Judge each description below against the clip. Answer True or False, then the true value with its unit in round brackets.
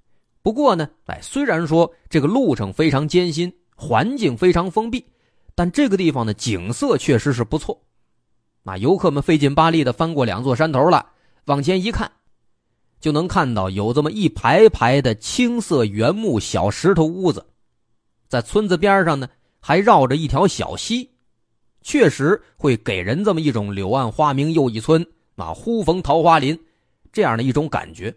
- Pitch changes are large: True (6.1 semitones)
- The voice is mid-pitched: True (150 Hz)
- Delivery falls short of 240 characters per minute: False (245 characters per minute)